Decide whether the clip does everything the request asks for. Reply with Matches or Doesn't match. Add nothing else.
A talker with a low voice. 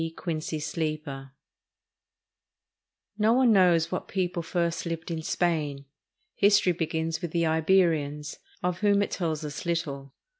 Doesn't match